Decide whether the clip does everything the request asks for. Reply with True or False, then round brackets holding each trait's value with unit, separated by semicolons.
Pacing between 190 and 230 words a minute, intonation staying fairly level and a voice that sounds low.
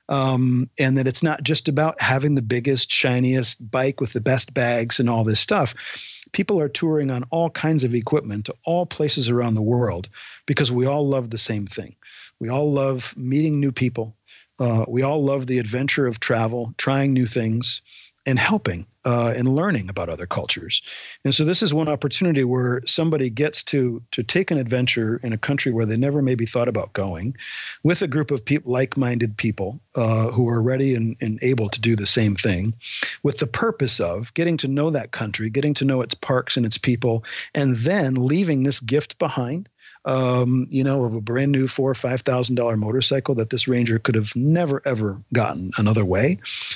False (200 wpm; 3.2 semitones; 125 Hz)